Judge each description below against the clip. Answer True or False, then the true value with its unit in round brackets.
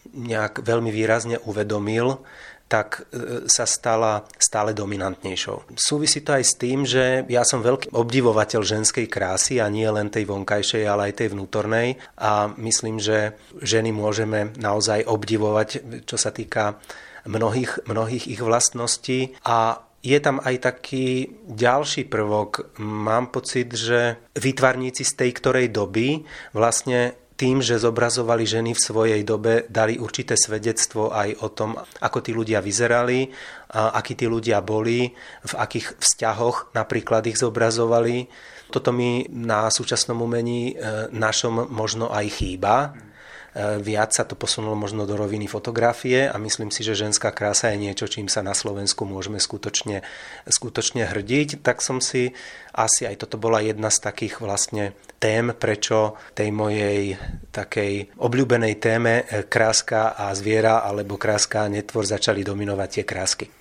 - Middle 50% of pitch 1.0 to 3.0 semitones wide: True (2.4 semitones)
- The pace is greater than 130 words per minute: True (140 wpm)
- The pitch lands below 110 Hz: False (115 Hz)